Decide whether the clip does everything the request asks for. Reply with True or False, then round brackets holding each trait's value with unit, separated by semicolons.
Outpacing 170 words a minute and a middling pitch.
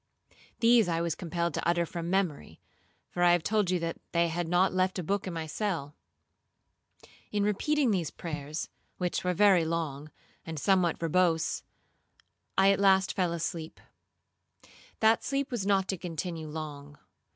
False (160 wpm; 175 Hz)